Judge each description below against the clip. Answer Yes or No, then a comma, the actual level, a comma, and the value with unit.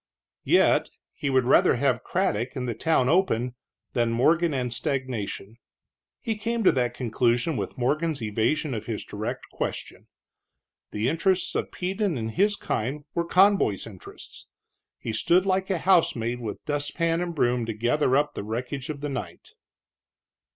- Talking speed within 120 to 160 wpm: Yes, average, 155 wpm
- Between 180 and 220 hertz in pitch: No, low, 135 Hz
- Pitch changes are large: Yes, wide, 6.2 semitones